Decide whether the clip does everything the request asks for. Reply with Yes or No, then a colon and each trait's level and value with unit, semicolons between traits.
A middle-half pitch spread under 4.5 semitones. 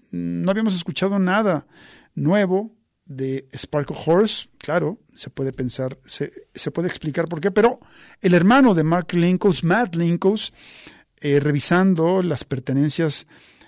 No: average, 5.0 semitones